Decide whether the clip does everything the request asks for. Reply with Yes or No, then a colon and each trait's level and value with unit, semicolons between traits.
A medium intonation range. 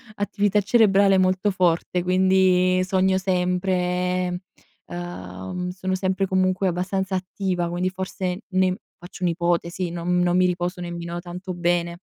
No: narrow, 1.2 semitones